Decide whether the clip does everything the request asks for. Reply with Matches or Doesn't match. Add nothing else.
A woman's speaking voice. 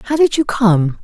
Matches